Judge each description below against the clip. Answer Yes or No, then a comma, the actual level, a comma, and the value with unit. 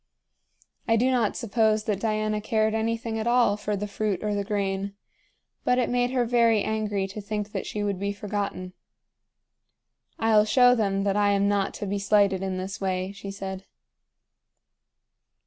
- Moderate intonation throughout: No, narrow, 1.9 semitones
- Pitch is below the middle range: No, high, 210 Hz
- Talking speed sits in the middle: Yes, average, 170 wpm